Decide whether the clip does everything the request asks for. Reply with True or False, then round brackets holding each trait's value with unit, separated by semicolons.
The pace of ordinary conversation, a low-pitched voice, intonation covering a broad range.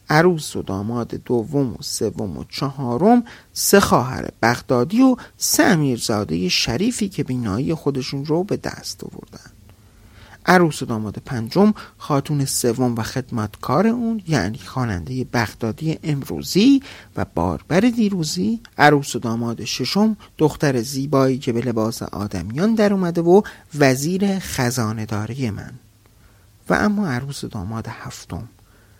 True (120 wpm; 130 Hz; 7.2 semitones)